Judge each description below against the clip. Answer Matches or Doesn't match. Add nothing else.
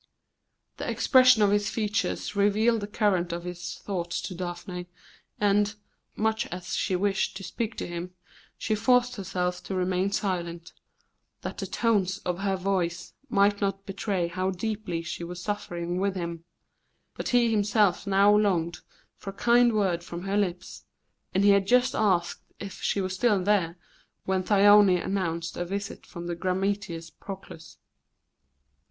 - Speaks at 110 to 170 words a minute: Matches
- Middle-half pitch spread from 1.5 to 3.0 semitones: Matches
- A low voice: Doesn't match